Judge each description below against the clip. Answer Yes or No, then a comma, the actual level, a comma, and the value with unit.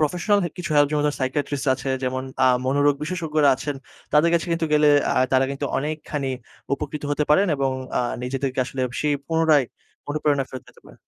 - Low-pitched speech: No, medium, 145 Hz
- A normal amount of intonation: No, narrow, 2.1 semitones